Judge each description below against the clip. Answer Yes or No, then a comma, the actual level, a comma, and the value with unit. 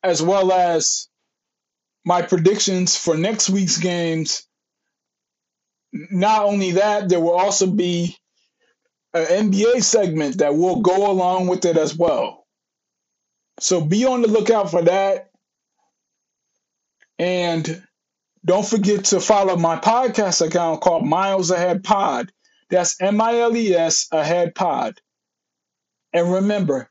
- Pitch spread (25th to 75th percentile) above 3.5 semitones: No, average, 2.9 semitones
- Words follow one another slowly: Yes, slow, 125 wpm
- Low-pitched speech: No, medium, 185 Hz